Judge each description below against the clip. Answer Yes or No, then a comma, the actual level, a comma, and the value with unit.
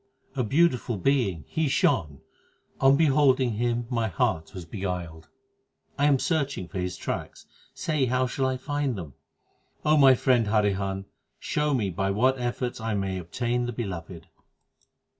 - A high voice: No, low, 120 Hz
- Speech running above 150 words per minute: No, average, 145 wpm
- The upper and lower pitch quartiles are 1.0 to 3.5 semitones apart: No, wide, 5.5 semitones